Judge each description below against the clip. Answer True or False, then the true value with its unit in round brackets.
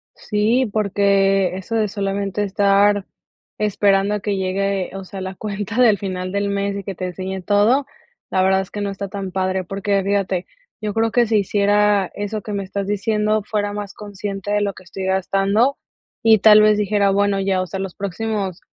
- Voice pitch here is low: False (200 Hz)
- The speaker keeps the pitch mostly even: True (1.3 semitones)